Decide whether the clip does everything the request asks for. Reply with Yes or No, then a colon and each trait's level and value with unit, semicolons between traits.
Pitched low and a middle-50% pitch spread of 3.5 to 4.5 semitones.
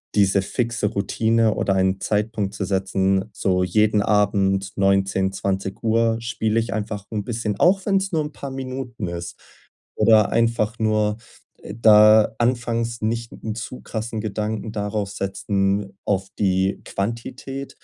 No: low, 105 Hz; average, 2.8 semitones